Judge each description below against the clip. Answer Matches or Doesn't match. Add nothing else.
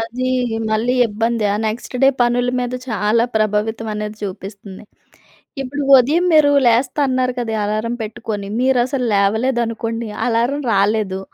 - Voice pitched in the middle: Doesn't match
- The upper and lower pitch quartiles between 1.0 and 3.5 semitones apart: Matches